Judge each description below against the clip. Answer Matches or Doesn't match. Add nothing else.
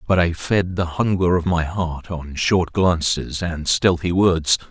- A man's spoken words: Matches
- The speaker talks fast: Doesn't match